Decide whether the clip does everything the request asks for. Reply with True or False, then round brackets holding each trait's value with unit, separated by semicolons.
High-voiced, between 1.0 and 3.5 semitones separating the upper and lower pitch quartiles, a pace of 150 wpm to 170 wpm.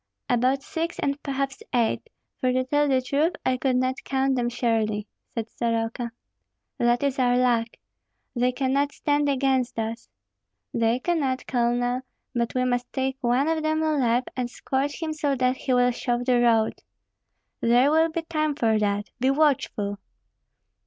True (255 Hz; 2.6 semitones; 160 wpm)